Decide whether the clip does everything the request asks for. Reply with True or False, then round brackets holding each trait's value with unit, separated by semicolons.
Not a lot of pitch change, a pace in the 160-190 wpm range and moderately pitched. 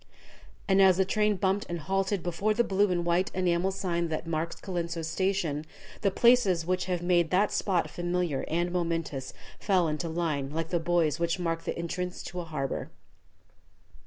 True (2.3 semitones; 175 wpm; 175 Hz)